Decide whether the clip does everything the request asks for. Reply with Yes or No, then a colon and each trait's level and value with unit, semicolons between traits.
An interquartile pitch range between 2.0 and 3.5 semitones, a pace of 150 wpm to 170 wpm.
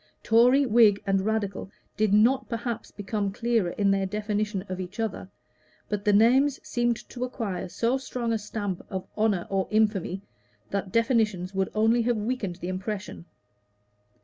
Yes: average, 3.1 semitones; average, 155 wpm